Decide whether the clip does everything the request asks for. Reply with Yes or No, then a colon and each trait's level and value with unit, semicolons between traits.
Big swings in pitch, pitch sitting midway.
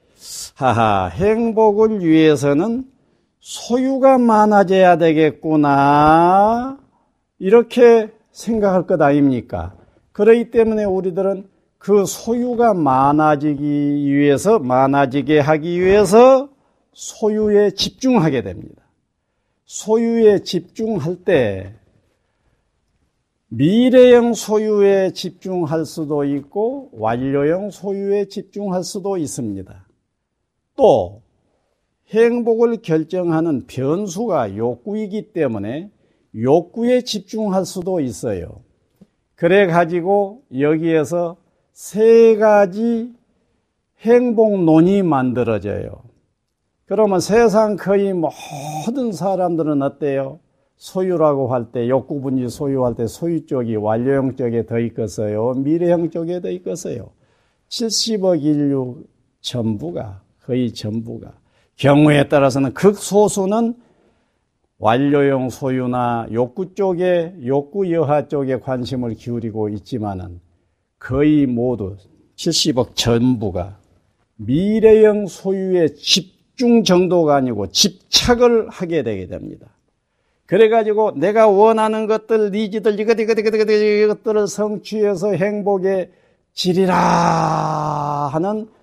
Yes: wide, 7.9 semitones; medium, 170 Hz